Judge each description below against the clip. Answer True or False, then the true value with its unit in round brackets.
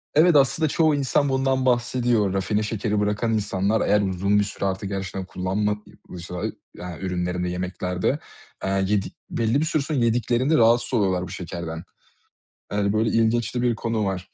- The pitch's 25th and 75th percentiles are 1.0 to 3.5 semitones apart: False (4.1 semitones)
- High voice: False (105 Hz)